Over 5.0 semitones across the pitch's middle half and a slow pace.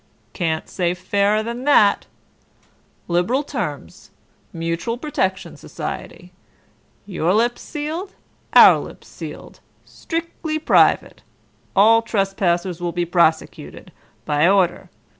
Yes: wide, 5.4 semitones; slow, 100 wpm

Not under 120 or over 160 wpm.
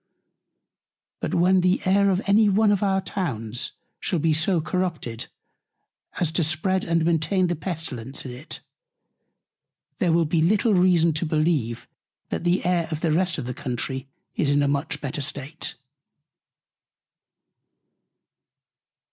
Yes: average, 140 wpm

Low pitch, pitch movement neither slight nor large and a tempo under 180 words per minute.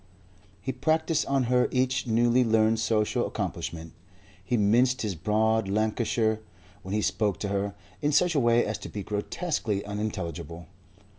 Yes: low, 110 Hz; average, 3.5 semitones; average, 150 wpm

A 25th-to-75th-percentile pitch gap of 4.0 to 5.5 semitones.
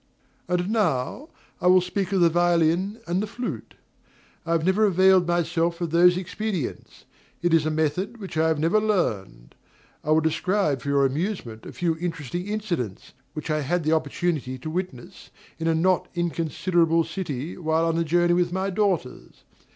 No: average, 2.8 semitones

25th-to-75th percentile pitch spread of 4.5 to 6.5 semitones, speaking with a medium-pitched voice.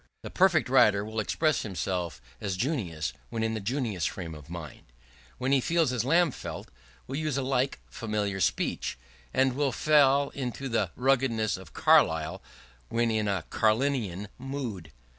No: wide, 5.5 semitones; low, 115 Hz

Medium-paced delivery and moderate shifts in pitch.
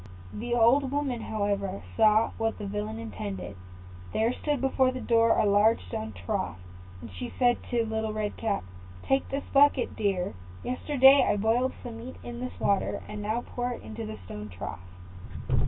Yes: average, 170 wpm; average, 4.4 semitones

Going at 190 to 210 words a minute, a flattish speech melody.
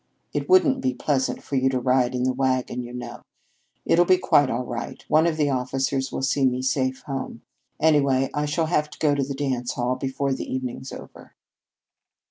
Yes: average, 200 wpm; narrow, 2.3 semitones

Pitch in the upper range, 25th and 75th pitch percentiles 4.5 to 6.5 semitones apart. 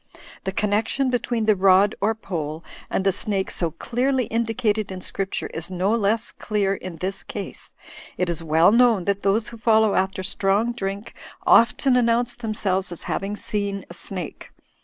No: high, 200 Hz; average, 3.1 semitones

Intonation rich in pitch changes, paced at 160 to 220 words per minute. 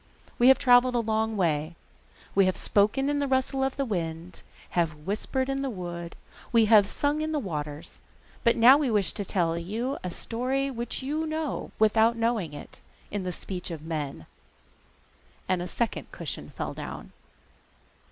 Yes: wide, 7.0 semitones; average, 170 wpm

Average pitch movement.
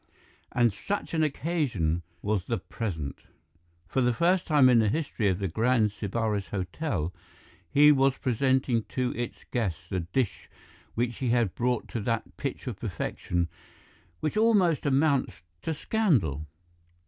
No: wide, 5.7 semitones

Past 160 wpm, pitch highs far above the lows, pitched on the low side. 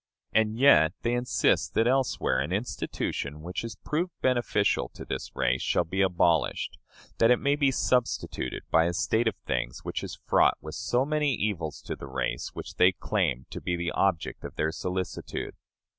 Yes: average, 180 wpm; wide, 7.2 semitones; very low, 95 Hz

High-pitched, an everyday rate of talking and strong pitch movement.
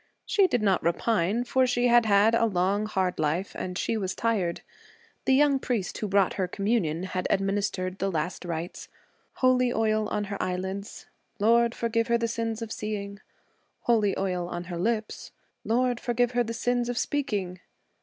No: high, 210 Hz; average, 175 wpm; average, 3.9 semitones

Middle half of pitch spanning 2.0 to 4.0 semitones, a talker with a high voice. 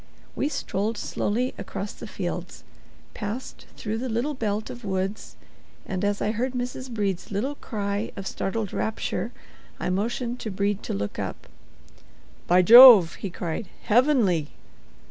Yes: average, 3.7 semitones; high, 210 Hz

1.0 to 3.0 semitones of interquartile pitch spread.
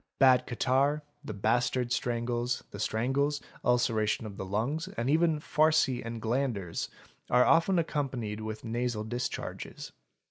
No: average, 3.9 semitones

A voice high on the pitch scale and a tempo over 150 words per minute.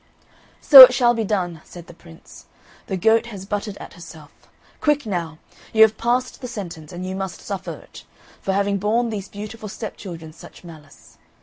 Yes: high, 200 Hz; average, 180 wpm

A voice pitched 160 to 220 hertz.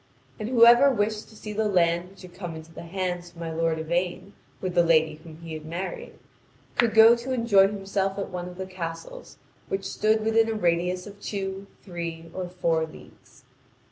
Yes: medium, 185 Hz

